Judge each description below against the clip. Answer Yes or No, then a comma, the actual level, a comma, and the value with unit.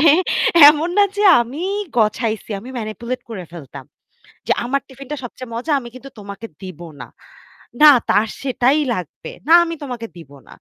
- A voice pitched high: Yes, high, 235 Hz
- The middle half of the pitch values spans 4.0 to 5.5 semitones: Yes, average, 4.9 semitones